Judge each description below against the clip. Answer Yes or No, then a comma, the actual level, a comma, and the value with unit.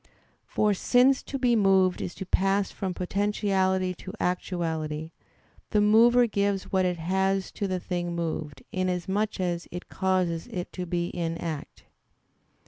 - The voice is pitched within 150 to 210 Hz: Yes, medium, 185 Hz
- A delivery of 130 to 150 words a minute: Yes, average, 145 wpm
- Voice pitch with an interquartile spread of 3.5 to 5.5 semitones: No, narrow, 2.4 semitones